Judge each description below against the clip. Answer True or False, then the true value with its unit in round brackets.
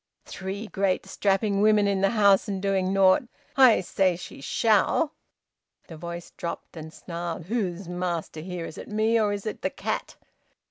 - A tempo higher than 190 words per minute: False (170 wpm)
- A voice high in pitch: True (195 Hz)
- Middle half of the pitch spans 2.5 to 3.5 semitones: True (3.0 semitones)